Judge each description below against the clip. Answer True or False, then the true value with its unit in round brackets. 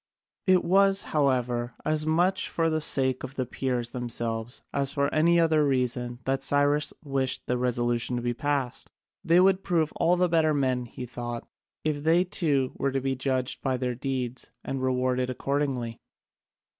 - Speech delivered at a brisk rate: False (170 wpm)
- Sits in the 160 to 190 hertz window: False (135 Hz)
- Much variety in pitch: False (3.8 semitones)